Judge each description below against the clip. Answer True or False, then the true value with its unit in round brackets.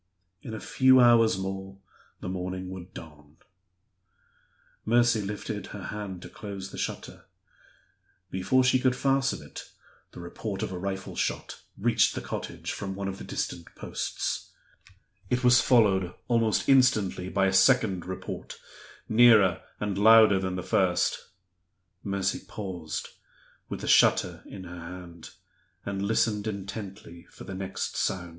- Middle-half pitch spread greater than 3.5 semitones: False (3.2 semitones)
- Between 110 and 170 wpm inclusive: True (140 wpm)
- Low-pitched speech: True (95 Hz)